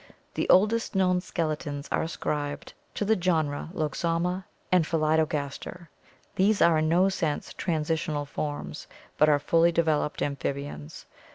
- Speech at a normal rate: No, slow, 130 wpm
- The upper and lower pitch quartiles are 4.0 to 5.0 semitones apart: No, average, 3.4 semitones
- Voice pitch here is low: No, medium, 160 Hz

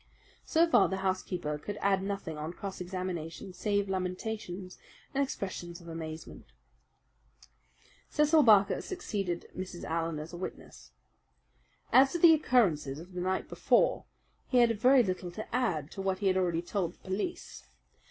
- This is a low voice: No, high, 190 Hz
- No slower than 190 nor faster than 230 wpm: No, average, 150 wpm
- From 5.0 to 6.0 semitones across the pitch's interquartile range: No, average, 3.7 semitones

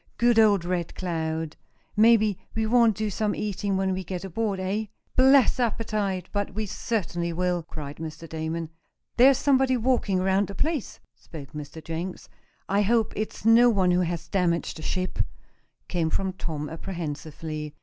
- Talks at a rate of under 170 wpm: Yes, average, 160 wpm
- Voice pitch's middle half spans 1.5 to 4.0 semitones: No, average, 4.7 semitones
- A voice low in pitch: No, high, 190 Hz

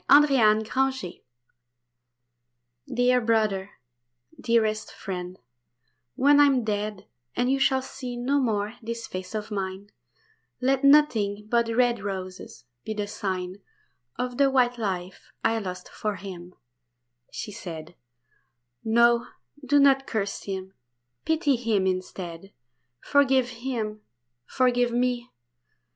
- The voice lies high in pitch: Yes, high, 225 Hz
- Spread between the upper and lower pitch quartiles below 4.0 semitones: No, average, 4.3 semitones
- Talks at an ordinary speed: No, slow, 115 wpm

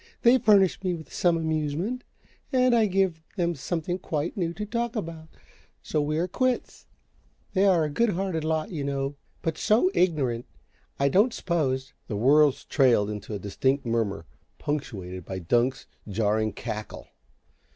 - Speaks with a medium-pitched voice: Yes, medium, 155 Hz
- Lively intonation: Yes, wide, 6.6 semitones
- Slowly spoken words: No, average, 160 wpm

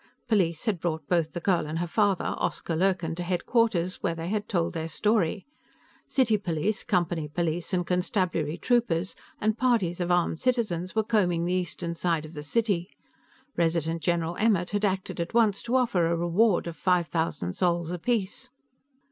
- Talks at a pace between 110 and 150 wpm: No, average, 175 wpm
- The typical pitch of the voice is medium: Yes, medium, 175 Hz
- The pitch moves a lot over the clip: No, average, 3.7 semitones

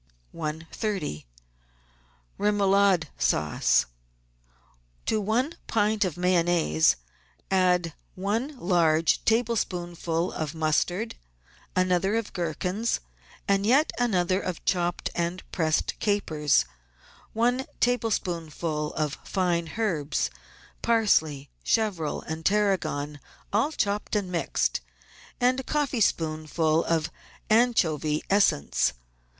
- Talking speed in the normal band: No, slow, 90 wpm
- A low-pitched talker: No, medium, 180 Hz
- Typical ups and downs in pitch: Yes, average, 4.9 semitones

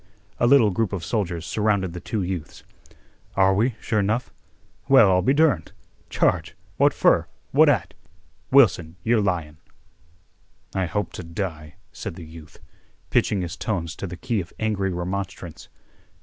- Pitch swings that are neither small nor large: Yes, average, 4.1 semitones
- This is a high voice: No, very low, 95 Hz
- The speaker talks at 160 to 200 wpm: No, average, 150 wpm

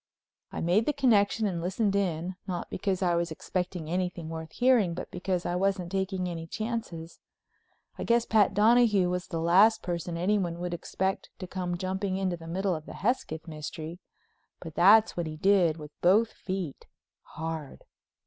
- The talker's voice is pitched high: No, medium, 180 Hz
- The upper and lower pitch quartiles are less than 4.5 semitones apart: Yes, average, 2.9 semitones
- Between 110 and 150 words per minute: No, average, 170 wpm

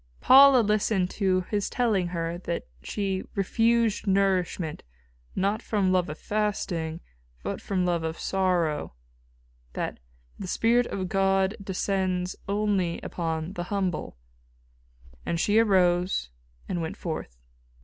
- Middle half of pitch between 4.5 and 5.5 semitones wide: No, average, 2.8 semitones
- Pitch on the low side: No, high, 190 Hz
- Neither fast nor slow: No, slow, 120 wpm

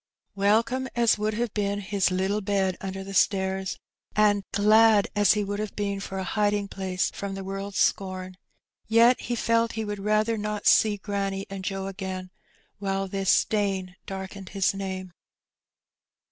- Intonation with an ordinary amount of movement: No, narrow, 1.7 semitones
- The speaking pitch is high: Yes, high, 200 Hz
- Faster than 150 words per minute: Yes, average, 160 wpm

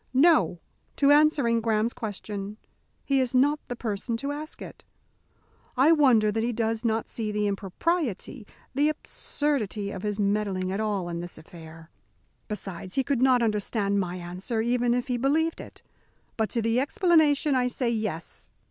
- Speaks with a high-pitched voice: Yes, high, 225 Hz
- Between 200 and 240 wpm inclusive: No, average, 165 wpm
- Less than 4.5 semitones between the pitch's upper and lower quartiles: No, average, 4.8 semitones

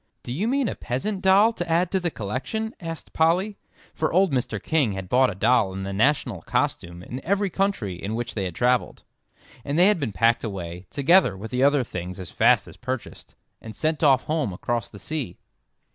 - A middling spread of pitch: No, wide, 9.0 semitones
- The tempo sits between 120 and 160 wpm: No, fast, 205 wpm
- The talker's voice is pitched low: Yes, low, 130 Hz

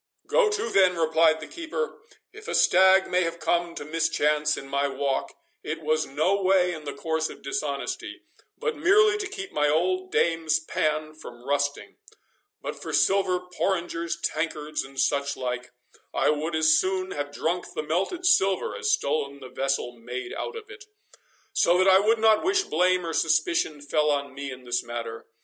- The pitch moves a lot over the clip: No, average, 4.7 semitones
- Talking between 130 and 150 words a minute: No, average, 180 wpm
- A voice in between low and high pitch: Yes, medium, 160 Hz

